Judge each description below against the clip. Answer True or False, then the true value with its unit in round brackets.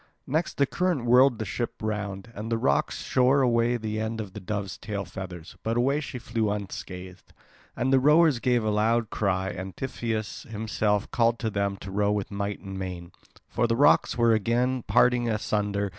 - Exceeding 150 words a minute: True (190 wpm)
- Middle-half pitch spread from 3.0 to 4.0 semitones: True (3.3 semitones)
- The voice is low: True (110 Hz)